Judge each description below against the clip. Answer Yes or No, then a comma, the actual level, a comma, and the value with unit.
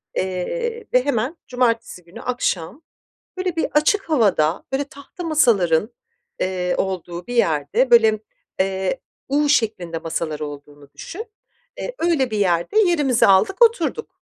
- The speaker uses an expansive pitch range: Yes, wide, 8.9 semitones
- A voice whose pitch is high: Yes, high, 230 Hz